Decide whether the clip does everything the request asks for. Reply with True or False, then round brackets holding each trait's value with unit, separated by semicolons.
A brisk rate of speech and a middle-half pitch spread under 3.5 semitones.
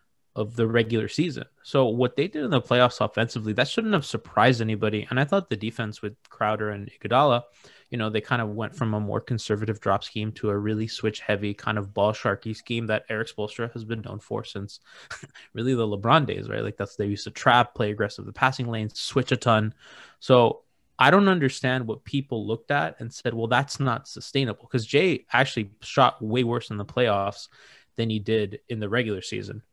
True (210 wpm; 2.9 semitones)